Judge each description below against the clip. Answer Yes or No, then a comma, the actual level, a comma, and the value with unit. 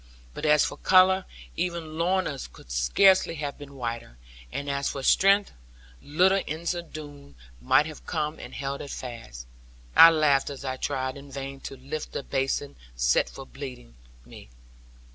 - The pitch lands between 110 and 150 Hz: Yes, medium, 140 Hz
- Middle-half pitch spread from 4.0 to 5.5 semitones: No, average, 3.5 semitones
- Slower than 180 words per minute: Yes, average, 160 wpm